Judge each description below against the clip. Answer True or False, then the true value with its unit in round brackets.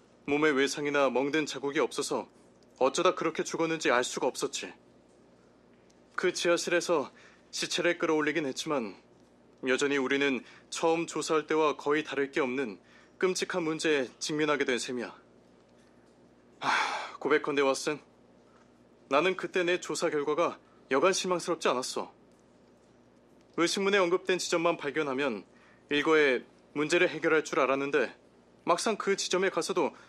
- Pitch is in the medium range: True (145 Hz)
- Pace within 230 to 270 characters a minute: False (285 characters per minute)